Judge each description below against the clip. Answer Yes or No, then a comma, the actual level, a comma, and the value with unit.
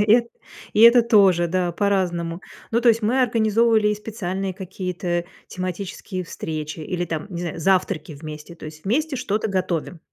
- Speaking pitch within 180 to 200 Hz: Yes, medium, 185 Hz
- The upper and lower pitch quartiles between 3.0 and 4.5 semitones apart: Yes, average, 4.0 semitones